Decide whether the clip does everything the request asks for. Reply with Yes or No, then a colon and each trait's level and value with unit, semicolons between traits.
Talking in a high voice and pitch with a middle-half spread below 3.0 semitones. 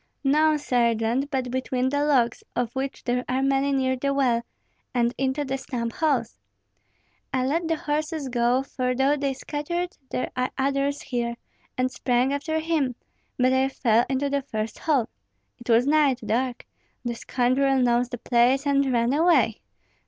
Yes: very high, 265 Hz; narrow, 2.5 semitones